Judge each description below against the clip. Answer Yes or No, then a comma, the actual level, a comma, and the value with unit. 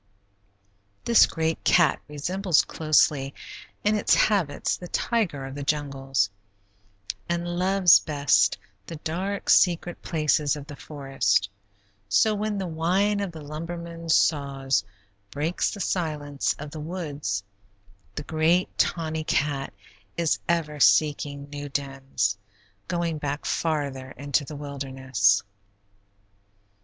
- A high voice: No, medium, 150 Hz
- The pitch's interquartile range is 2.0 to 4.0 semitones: Yes, average, 3.5 semitones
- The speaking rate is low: Yes, slow, 115 wpm